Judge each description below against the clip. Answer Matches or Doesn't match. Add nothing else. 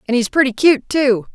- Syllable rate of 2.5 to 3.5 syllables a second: Doesn't match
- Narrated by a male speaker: Doesn't match